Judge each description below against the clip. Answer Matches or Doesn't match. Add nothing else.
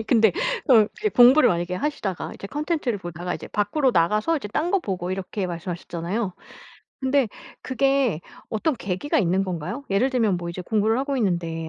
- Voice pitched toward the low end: Doesn't match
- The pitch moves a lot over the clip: Matches